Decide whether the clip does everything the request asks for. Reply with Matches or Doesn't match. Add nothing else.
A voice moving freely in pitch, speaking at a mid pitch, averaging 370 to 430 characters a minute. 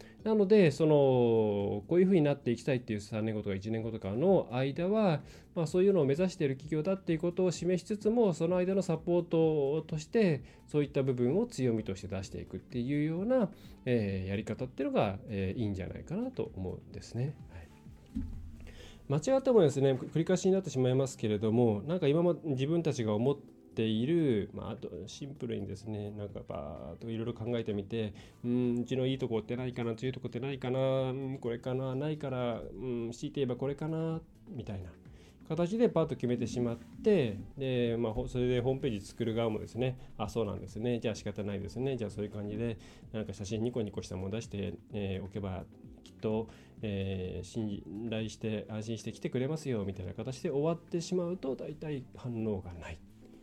Doesn't match